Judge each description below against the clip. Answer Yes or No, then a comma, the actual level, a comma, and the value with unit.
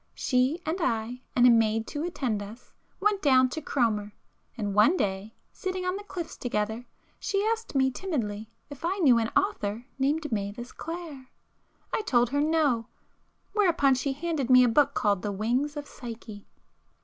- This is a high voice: Yes, very high, 255 Hz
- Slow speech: No, average, 160 wpm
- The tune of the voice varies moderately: No, wide, 6.2 semitones